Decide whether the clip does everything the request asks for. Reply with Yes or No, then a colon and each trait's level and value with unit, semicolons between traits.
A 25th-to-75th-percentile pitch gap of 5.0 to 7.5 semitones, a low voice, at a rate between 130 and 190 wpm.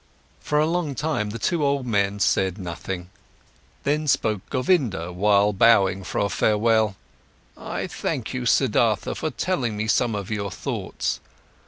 Yes: wide, 5.4 semitones; low, 110 Hz; average, 150 wpm